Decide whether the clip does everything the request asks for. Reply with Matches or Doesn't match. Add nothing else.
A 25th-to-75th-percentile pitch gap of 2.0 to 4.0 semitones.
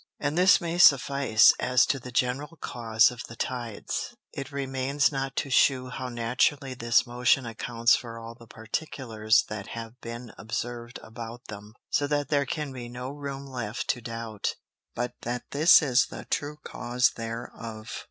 Matches